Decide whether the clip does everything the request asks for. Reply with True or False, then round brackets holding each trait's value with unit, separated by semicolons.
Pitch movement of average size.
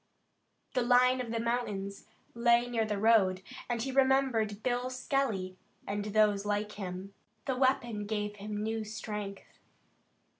True (3.0 semitones)